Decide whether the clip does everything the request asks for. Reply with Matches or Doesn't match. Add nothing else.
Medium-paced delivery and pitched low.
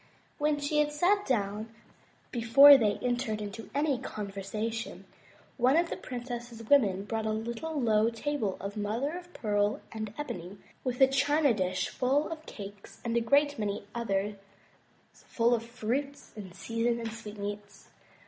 Doesn't match